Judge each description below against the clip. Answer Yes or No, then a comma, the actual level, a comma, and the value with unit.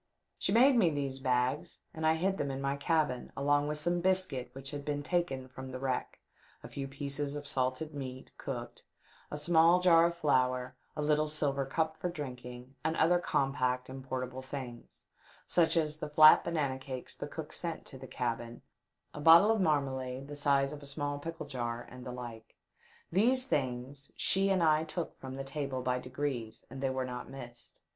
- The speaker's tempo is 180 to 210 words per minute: Yes, average, 195 wpm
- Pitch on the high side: No, medium, 140 Hz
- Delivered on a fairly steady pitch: No, average, 3.6 semitones